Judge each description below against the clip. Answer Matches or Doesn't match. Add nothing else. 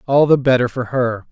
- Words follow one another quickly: Matches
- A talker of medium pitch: Doesn't match